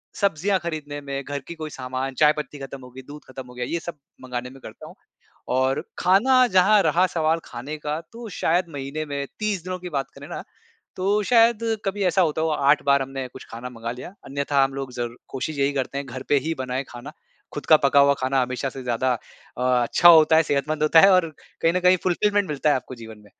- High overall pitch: No, medium, 145 Hz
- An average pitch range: Yes, average, 4.7 semitones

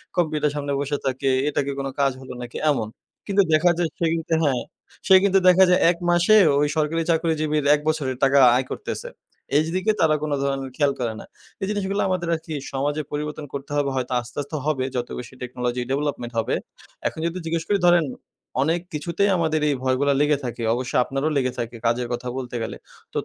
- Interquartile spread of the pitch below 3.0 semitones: No, average, 3.9 semitones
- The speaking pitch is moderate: Yes, medium, 145 Hz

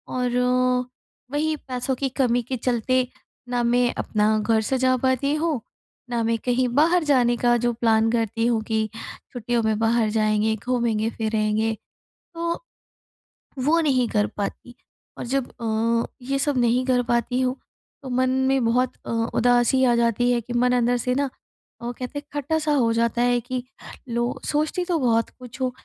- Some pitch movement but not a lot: No, narrow, 2.1 semitones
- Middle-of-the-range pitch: No, high, 245 Hz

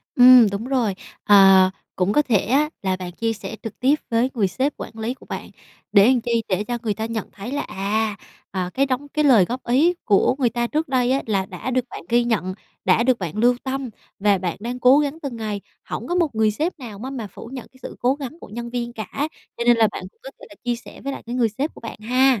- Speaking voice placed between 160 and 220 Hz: No, high, 235 Hz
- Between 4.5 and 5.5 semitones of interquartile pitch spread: No, average, 3.7 semitones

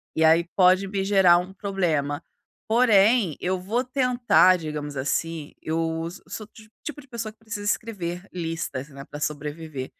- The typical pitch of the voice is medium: Yes, medium, 180 Hz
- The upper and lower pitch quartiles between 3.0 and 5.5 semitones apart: Yes, average, 4.9 semitones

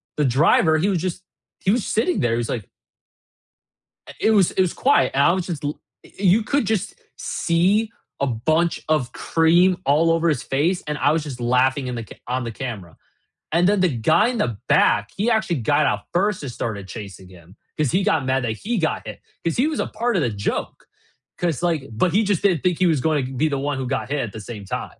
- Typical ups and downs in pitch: No, wide, 6.2 semitones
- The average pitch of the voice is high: No, medium, 160 Hz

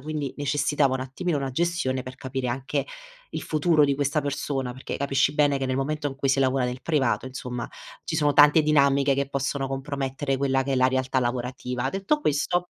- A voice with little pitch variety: Yes, narrow, 2.0 semitones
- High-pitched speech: No, low, 135 Hz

